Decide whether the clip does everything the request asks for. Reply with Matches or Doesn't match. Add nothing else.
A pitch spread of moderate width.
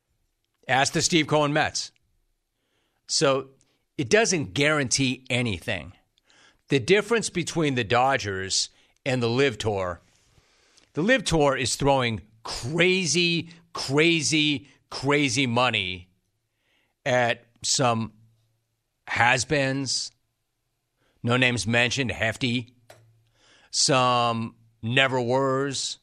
Matches